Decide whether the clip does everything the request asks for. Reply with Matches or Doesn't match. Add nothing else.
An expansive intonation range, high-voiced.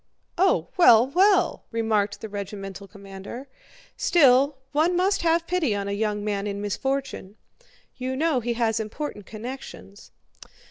Matches